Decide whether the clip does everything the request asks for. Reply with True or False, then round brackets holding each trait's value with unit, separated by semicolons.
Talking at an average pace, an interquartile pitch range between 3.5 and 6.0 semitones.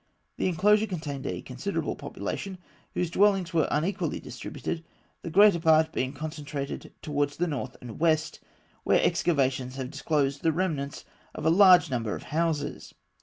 True (150 wpm; 3.9 semitones)